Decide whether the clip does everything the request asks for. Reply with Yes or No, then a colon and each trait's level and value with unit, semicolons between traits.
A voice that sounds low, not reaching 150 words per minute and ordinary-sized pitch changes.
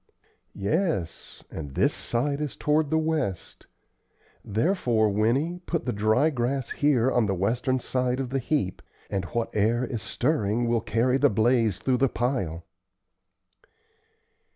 Yes: low, 120 Hz; average, 140 wpm; average, 4.5 semitones